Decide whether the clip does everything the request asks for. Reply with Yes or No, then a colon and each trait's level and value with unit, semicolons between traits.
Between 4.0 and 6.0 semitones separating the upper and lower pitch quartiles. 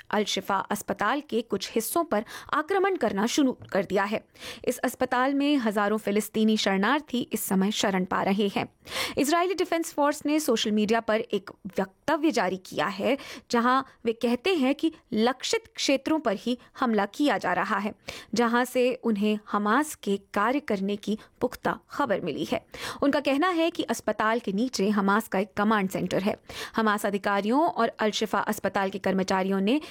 Yes: average, 4.7 semitones